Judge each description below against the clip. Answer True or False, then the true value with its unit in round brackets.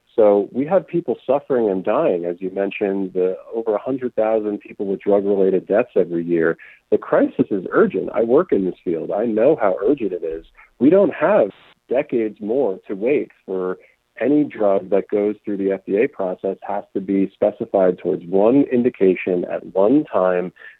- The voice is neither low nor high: False (100 Hz)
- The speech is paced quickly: False (175 wpm)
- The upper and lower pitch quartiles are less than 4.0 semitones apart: True (2.8 semitones)